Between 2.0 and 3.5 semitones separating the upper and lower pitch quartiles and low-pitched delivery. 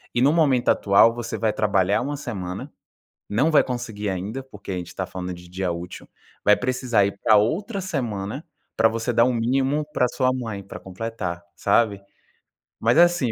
No: average, 4.6 semitones; low, 115 Hz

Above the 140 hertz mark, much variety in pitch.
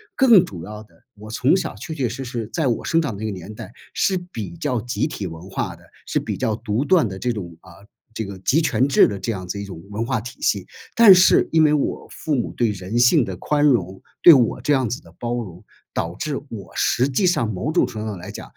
No: low, 115 Hz; wide, 6.1 semitones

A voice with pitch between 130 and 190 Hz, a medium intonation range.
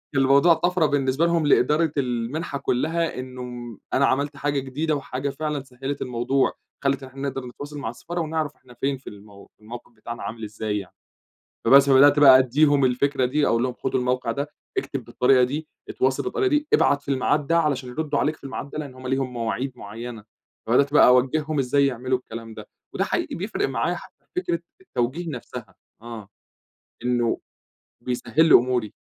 Yes: low, 135 Hz; average, 3.0 semitones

